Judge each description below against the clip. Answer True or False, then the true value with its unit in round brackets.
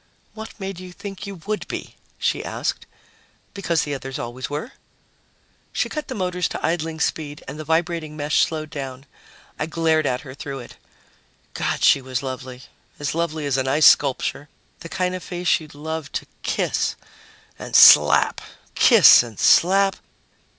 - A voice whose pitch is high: False (155 Hz)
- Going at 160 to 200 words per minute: True (165 wpm)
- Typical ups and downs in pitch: True (4.3 semitones)